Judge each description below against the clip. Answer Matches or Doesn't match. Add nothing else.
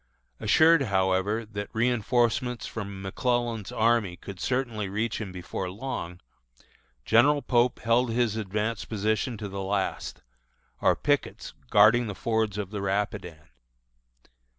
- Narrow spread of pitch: Doesn't match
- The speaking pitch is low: Matches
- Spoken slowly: Matches